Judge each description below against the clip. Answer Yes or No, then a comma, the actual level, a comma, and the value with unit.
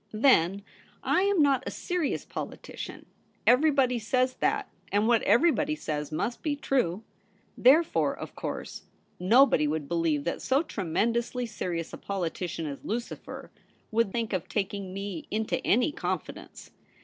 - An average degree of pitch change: No, wide, 6.9 semitones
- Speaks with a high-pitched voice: Yes, high, 225 Hz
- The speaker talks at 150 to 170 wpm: No, average, 140 wpm